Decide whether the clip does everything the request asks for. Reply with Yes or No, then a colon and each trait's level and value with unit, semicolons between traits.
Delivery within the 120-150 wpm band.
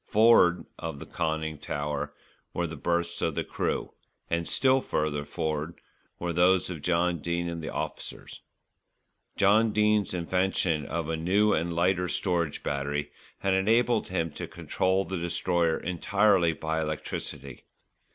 Yes: average, 140 wpm